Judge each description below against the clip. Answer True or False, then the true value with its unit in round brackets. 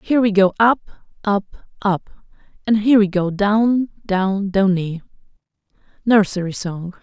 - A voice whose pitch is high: True (200 Hz)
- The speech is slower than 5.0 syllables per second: True (4.6 syllables/s)